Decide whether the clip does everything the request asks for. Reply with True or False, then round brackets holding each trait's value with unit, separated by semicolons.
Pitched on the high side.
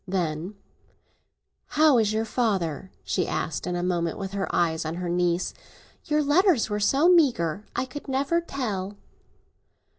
True (205 Hz)